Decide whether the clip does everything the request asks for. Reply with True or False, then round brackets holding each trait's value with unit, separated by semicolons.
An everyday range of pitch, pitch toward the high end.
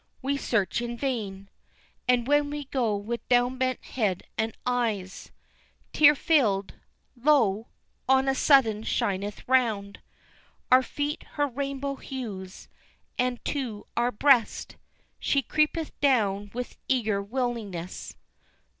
True (4.6 semitones; 245 Hz)